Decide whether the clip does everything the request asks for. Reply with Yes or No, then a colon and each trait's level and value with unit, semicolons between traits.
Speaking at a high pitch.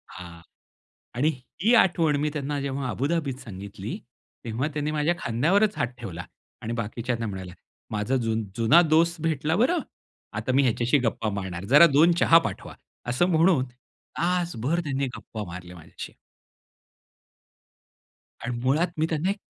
No: low, 135 Hz